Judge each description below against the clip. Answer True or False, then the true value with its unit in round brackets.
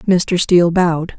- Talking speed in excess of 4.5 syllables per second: False (4.4 syllables/s)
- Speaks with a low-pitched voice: False (175 Hz)